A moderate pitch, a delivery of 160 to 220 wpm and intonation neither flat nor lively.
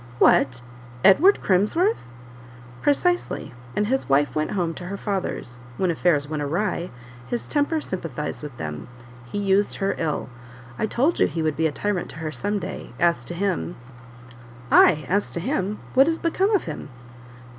No: medium, 180 Hz; average, 170 wpm; wide, 5.9 semitones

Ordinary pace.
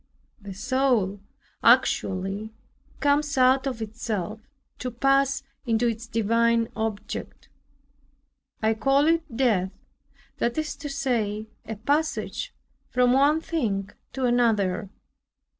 No: slow, 110 wpm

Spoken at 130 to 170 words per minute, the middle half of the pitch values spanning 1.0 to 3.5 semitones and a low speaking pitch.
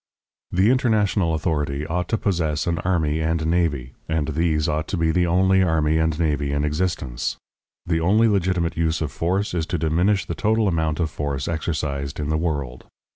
No: average, 180 wpm; average, 2.7 semitones; very low, 80 Hz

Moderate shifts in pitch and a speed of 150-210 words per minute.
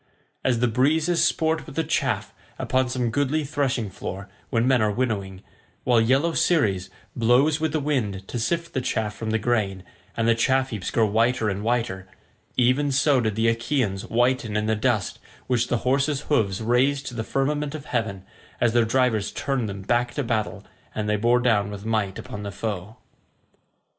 Yes: average, 3.9 semitones; average, 180 wpm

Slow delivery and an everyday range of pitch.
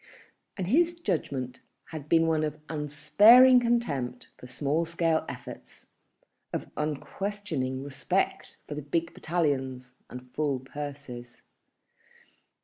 Yes: slow, 110 wpm; average, 4.3 semitones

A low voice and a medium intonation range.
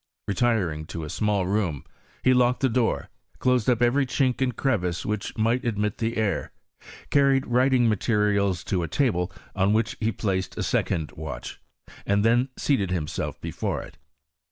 Yes: low, 110 Hz; average, 4.6 semitones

